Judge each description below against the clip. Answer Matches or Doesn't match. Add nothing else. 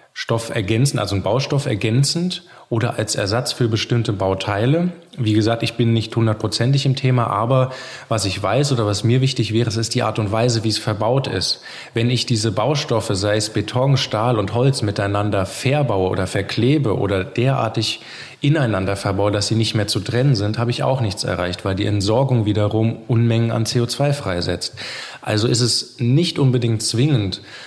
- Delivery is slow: Doesn't match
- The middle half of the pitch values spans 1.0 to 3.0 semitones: Doesn't match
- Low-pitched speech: Matches